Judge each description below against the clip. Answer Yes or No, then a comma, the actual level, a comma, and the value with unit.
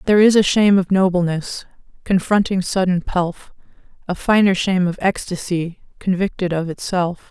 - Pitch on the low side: No, medium, 185 Hz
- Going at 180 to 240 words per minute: No, average, 140 wpm